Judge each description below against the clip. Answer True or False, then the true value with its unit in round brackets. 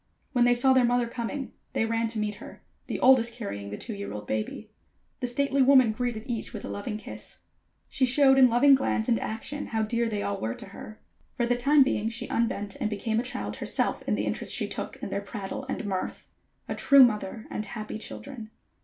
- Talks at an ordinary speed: False (220 wpm)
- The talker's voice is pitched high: True (230 Hz)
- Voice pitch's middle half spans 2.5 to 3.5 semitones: True (3.0 semitones)